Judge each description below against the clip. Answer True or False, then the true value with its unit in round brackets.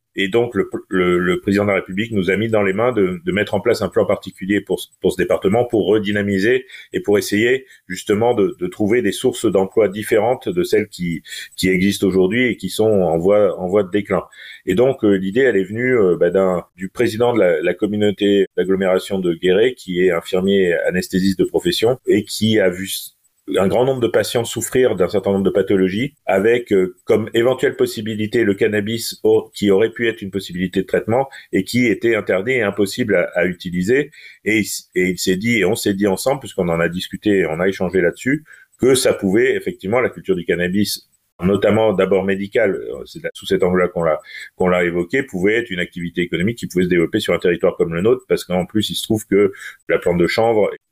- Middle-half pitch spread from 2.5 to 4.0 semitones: False (4.5 semitones)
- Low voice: True (100 Hz)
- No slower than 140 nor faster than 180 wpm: False (220 wpm)